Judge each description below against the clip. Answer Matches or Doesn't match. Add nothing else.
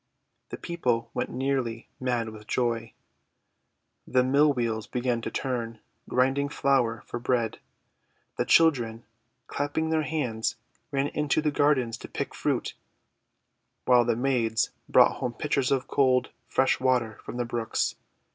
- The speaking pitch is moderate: Doesn't match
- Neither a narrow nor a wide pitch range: Matches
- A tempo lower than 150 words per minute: Matches